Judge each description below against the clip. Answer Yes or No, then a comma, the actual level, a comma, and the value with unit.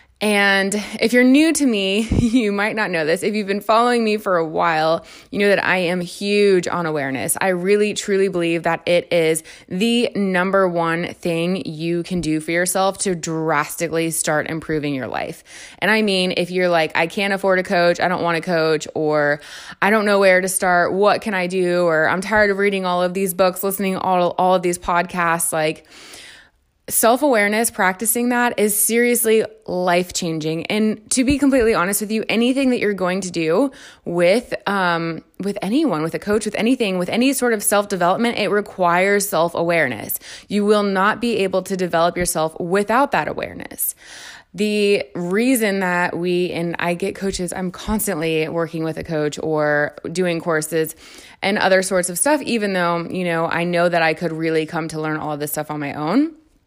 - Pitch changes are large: No, average, 3.7 semitones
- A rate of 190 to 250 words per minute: Yes, average, 195 wpm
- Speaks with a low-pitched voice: No, medium, 185 Hz